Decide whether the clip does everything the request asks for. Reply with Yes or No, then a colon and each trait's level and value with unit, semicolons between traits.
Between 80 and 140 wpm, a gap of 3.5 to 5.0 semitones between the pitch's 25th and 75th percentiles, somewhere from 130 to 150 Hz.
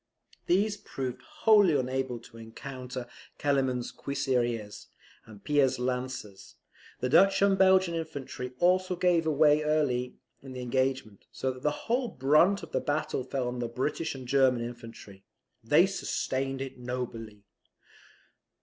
Yes: slow, 135 wpm; average, 4.2 semitones; low, 135 Hz